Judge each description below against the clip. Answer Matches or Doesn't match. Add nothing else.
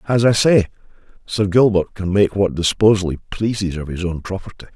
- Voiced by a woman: Doesn't match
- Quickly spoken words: Doesn't match